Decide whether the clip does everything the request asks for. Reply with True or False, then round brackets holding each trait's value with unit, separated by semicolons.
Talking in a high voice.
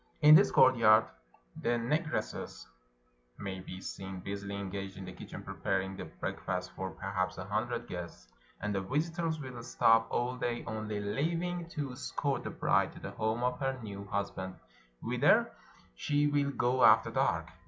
False (110 Hz)